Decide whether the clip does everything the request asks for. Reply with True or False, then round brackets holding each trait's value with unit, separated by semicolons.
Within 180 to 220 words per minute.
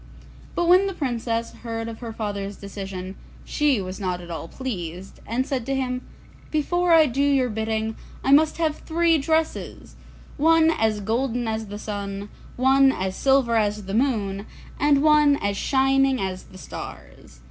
False (165 wpm)